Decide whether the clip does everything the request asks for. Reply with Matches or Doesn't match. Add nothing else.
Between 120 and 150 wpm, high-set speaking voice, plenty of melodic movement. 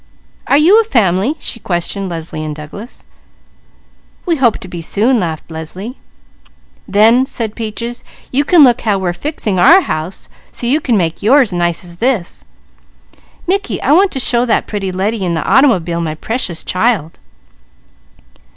Doesn't match